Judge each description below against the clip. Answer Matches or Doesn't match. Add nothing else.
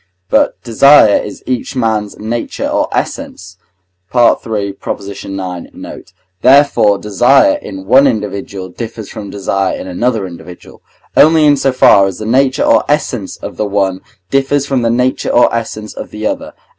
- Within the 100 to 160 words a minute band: Matches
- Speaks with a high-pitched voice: Doesn't match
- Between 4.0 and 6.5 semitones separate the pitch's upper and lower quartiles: Matches